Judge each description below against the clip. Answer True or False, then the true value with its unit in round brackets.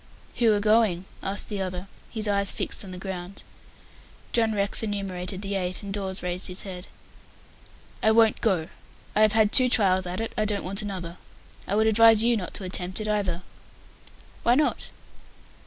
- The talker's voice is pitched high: True (200 Hz)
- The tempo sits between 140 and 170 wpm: False (180 wpm)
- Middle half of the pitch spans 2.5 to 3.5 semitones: True (2.8 semitones)